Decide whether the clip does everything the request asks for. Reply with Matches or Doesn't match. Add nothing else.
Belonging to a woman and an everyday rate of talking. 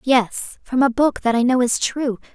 Doesn't match